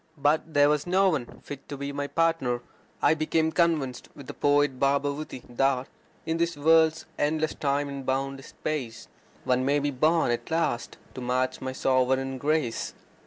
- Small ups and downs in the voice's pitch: No, average, 3.0 semitones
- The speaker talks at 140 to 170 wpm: Yes, average, 165 wpm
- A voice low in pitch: No, medium, 145 Hz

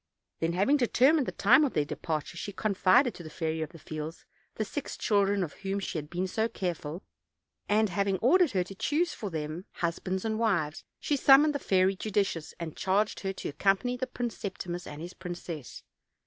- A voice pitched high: Yes, high, 195 Hz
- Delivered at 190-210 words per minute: Yes, average, 195 wpm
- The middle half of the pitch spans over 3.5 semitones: Yes, average, 4.8 semitones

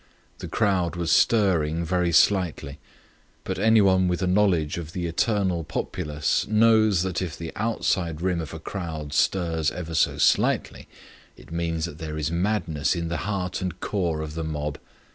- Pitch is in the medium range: No, very low, 85 Hz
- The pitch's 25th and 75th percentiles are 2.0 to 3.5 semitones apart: Yes, average, 2.9 semitones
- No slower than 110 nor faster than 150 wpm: No, average, 165 wpm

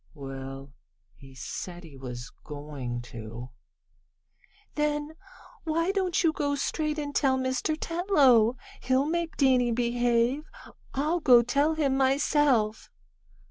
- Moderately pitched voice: No, very high, 260 Hz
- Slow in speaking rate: Yes, slow, 115 wpm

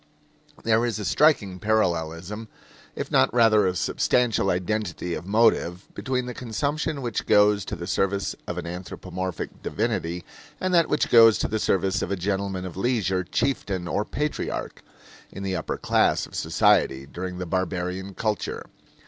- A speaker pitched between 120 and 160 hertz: No, low, 100 Hz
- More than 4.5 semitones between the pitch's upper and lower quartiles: No, average, 3.8 semitones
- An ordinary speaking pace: Yes, average, 155 wpm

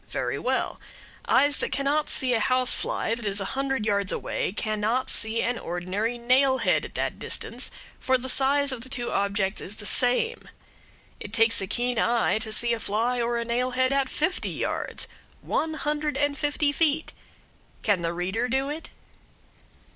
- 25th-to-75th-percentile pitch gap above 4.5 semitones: No, average, 4.1 semitones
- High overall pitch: Yes, high, 245 Hz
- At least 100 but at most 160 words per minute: No, average, 175 wpm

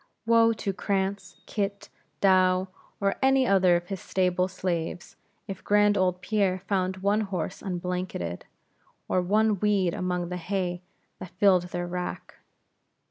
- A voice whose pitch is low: No, medium, 185 Hz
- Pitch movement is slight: Yes, narrow, 1.9 semitones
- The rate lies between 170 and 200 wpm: No, slow, 135 wpm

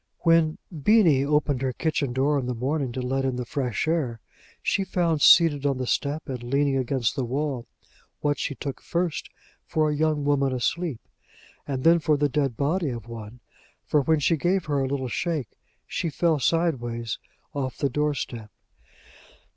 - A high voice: No, medium, 140 Hz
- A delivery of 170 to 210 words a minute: Yes, average, 180 wpm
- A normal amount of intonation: Yes, average, 3.4 semitones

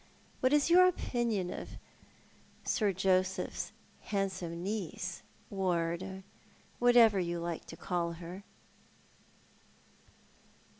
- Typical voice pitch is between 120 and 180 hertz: No, high, 190 Hz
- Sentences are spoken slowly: Yes, slow, 100 wpm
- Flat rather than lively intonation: No, average, 3.9 semitones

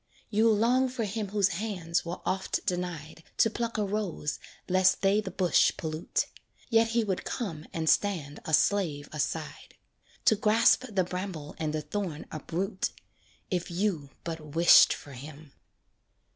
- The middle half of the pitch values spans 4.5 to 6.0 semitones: Yes, average, 4.8 semitones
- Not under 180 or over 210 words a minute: No, average, 150 wpm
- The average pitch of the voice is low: No, medium, 185 Hz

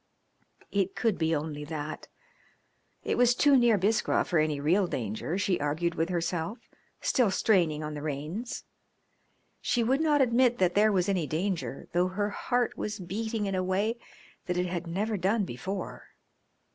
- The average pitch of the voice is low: No, medium, 185 Hz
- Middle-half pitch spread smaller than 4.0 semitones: No, average, 5.2 semitones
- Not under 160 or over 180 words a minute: Yes, average, 165 wpm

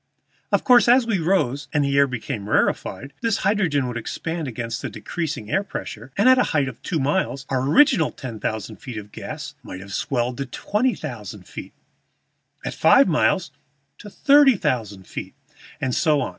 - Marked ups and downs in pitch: Yes, wide, 7.9 semitones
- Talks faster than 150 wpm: Yes, average, 185 wpm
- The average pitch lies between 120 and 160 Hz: Yes, medium, 140 Hz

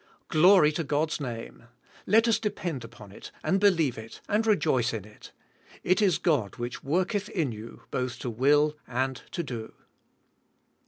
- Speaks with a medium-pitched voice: Yes, medium, 145 Hz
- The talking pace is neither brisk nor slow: Yes, average, 165 wpm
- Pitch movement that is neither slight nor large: No, wide, 7.4 semitones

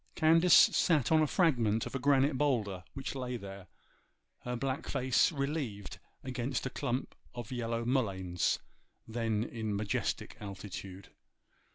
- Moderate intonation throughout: Yes, average, 4.7 semitones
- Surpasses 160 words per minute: No, slow, 135 wpm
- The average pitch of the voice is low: Yes, low, 120 Hz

